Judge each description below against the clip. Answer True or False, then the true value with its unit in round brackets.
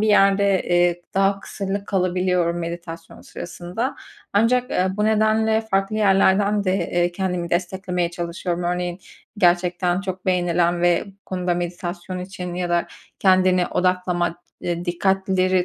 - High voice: False (180 Hz)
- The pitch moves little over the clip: True (1.9 semitones)